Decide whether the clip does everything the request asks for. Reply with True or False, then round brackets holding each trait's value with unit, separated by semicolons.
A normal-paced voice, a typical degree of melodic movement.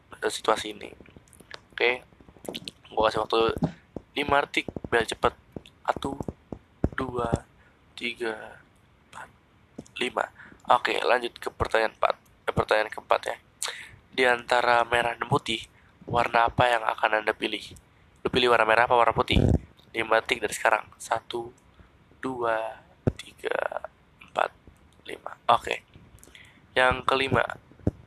False (120 wpm; 2.0 semitones)